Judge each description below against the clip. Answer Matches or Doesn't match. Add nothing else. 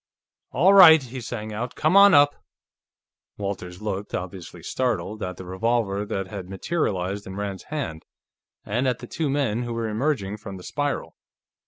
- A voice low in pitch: Matches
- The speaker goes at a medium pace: Matches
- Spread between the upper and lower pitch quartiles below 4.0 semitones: Doesn't match